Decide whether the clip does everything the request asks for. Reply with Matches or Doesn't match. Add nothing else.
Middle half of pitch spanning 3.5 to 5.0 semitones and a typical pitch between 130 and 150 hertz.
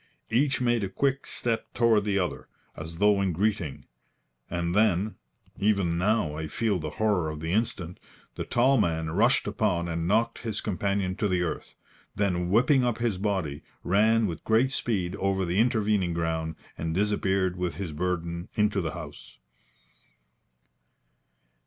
Doesn't match